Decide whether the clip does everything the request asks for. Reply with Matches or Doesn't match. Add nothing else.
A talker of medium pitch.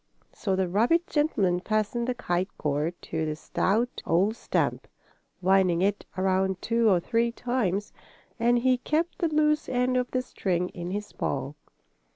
Doesn't match